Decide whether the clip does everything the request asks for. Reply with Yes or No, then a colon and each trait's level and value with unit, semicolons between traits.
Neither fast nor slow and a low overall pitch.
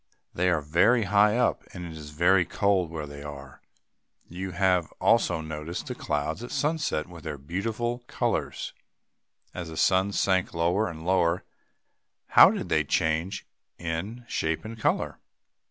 Yes: average, 155 wpm; very low, 90 Hz